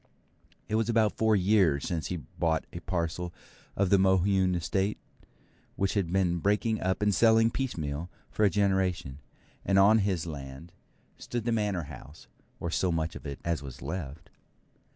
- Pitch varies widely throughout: No, average, 3.9 semitones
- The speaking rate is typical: Yes, average, 165 wpm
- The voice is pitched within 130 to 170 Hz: No, very low, 90 Hz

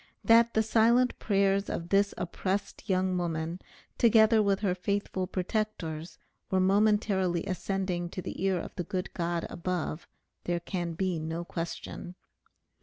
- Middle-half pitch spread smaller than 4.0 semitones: Yes, average, 2.7 semitones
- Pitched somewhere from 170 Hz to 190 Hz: Yes, medium, 185 Hz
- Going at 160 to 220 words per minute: No, average, 140 wpm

